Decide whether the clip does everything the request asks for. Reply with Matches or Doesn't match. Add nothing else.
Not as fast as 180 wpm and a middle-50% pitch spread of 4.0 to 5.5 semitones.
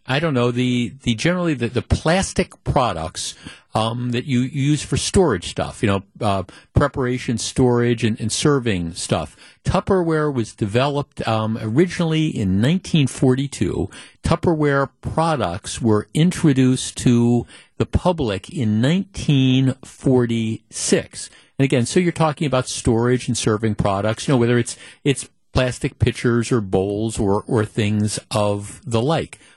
Matches